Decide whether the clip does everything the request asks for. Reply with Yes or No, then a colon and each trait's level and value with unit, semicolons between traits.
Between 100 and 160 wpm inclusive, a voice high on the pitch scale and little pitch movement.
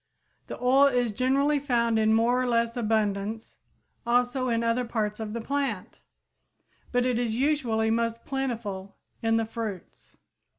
Yes: average, 140 wpm; high, 235 Hz; narrow, 2.2 semitones